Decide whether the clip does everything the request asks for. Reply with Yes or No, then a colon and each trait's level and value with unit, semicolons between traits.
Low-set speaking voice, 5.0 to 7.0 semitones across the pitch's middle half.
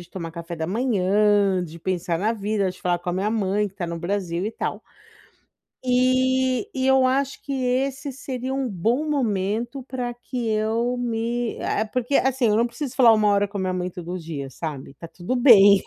No: high, 215 Hz; wide, 5.4 semitones